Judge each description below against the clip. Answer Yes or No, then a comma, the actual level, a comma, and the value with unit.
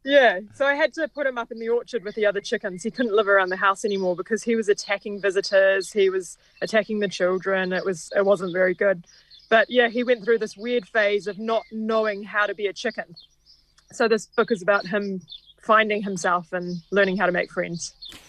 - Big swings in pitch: No, average, 3.0 semitones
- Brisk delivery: Yes, fast, 225 wpm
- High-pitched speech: Yes, high, 205 Hz